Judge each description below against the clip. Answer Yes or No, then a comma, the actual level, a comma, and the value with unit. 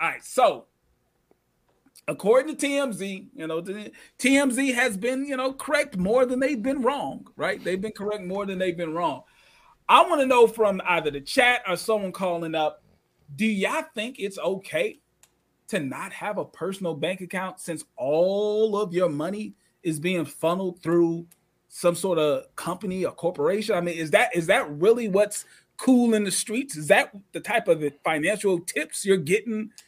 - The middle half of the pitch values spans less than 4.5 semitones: No, average, 4.8 semitones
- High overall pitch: Yes, high, 195 Hz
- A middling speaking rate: Yes, average, 180 wpm